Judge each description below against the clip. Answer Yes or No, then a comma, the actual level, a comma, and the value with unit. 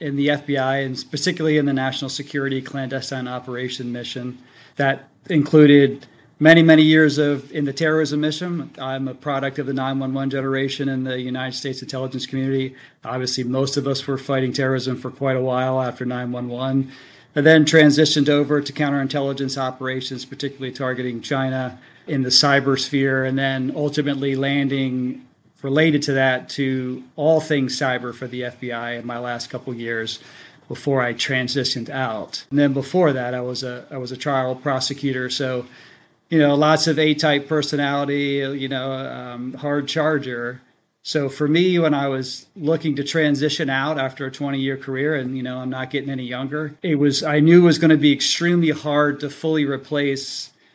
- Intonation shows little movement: Yes, narrow, 2.1 semitones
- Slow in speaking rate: No, average, 175 wpm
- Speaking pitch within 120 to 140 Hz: Yes, low, 135 Hz